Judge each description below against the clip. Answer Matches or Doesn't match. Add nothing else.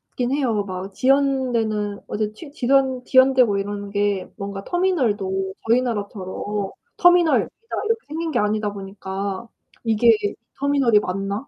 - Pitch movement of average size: Matches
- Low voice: Doesn't match